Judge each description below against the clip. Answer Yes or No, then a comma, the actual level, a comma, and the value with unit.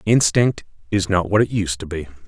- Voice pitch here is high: No, low, 100 Hz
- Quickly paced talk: Yes, fast, 210 wpm